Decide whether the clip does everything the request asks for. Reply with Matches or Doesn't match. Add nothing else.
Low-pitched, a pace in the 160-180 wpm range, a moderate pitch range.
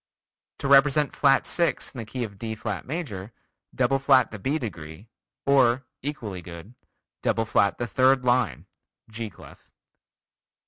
Doesn't match